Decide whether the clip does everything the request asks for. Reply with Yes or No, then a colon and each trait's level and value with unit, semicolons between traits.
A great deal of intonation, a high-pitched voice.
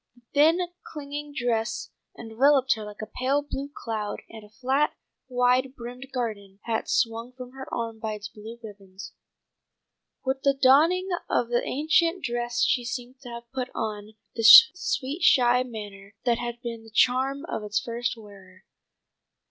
No: average, 3.3 semitones; high, 240 Hz